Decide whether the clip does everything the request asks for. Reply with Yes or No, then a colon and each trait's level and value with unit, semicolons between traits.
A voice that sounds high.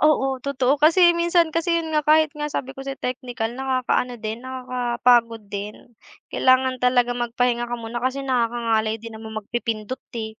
Yes: very high, 250 Hz